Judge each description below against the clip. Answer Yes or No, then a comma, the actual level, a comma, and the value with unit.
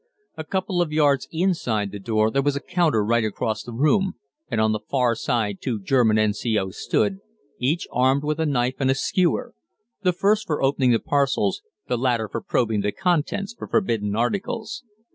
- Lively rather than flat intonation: Yes, wide, 6.7 semitones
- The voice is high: No, low, 130 Hz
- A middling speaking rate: Yes, average, 185 wpm